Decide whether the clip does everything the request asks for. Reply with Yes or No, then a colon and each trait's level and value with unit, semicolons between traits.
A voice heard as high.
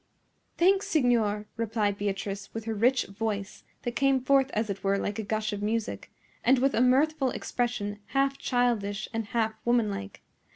Yes: high, 225 Hz